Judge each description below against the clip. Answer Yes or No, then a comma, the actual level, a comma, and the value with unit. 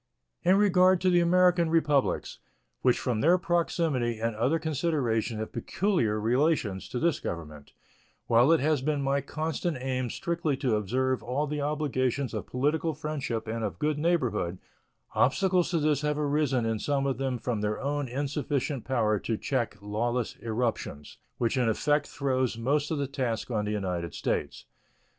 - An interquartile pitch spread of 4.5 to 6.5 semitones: Yes, average, 4.9 semitones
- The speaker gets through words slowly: No, average, 165 wpm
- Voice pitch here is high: No, low, 135 Hz